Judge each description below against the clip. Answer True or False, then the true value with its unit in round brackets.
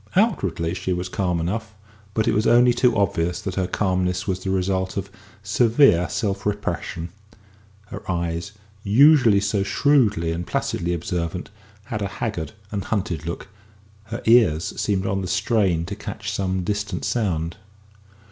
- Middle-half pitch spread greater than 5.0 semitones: False (3.5 semitones)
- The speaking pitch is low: True (95 Hz)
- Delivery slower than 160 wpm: True (150 wpm)